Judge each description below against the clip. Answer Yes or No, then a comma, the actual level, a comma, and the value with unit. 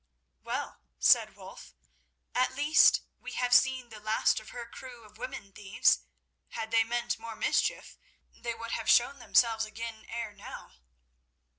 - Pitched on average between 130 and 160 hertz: No, high, 230 Hz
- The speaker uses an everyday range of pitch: No, narrow, 2.1 semitones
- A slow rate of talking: No, average, 155 wpm